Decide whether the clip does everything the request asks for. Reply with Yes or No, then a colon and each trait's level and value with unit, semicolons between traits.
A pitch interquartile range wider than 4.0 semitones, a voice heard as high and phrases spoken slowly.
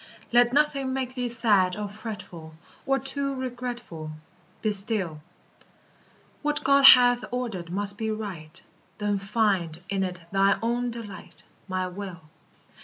Yes: average, 4.8 semitones; high, 215 Hz; slow, 130 wpm